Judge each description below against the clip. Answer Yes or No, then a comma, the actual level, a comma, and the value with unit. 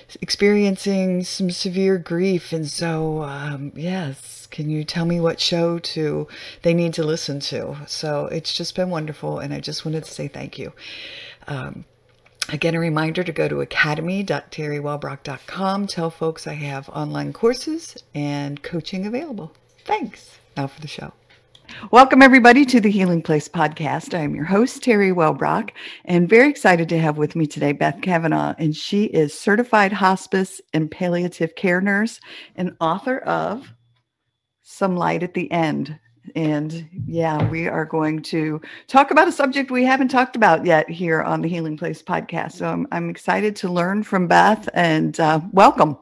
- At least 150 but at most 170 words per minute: Yes, average, 165 wpm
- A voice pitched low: No, medium, 165 Hz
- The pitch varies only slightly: No, average, 4.2 semitones